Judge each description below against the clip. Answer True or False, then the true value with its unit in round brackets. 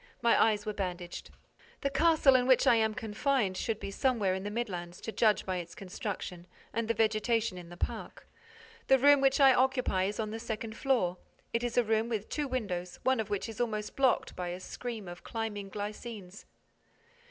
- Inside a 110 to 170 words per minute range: False (200 wpm)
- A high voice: True (220 Hz)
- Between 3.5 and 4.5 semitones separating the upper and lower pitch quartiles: True (4.0 semitones)